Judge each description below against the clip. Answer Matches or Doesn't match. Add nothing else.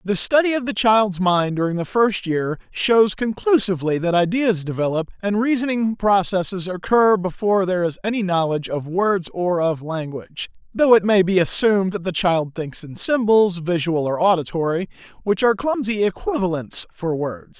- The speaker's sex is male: Matches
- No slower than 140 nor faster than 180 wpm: Matches